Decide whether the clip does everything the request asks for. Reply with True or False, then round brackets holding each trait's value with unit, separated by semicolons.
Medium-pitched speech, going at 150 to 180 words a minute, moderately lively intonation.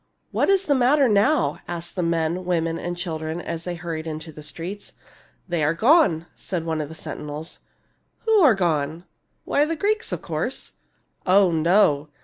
False (170 Hz; 200 wpm; 4.8 semitones)